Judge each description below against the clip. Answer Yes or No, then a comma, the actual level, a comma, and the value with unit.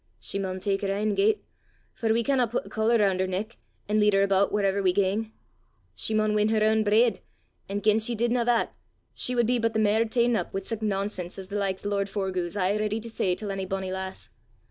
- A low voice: No, high, 210 Hz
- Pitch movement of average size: No, narrow, 2.3 semitones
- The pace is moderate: No, fast, 240 wpm